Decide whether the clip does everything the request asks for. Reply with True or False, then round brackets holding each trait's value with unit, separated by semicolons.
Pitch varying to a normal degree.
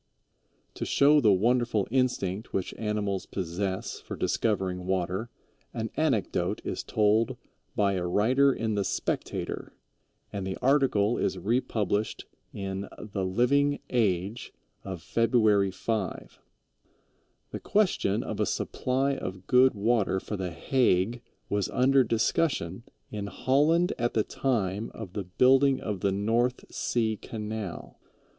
True (4.5 semitones)